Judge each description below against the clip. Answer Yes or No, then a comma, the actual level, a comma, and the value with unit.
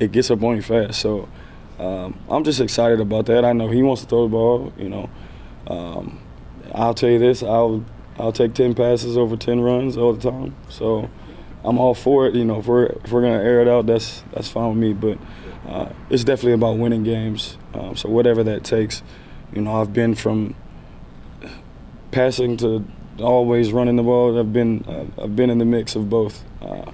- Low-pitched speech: Yes, low, 115 Hz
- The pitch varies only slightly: Yes, narrow, 1.7 semitones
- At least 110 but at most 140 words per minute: No, fast, 205 wpm